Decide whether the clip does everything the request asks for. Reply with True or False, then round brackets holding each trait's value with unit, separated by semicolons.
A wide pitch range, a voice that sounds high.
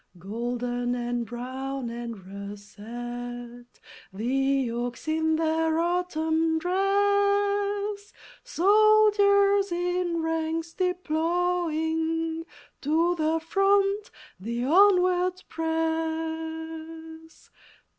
True (6.5 semitones; 320 Hz)